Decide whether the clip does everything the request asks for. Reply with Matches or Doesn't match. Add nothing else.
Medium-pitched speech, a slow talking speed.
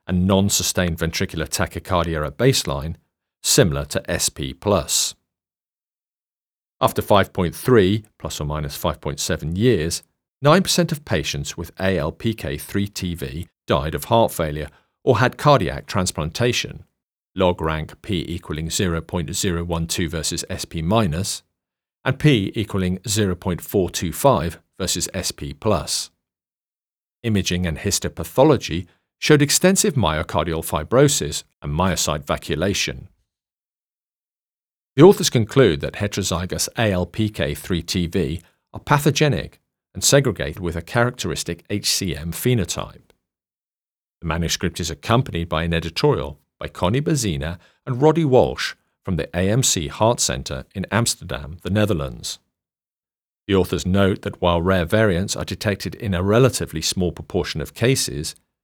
Doesn't match